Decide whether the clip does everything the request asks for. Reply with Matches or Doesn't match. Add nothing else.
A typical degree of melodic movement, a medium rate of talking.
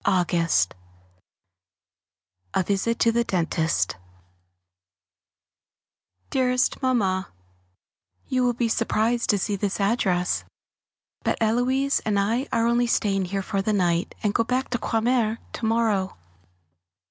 Doesn't match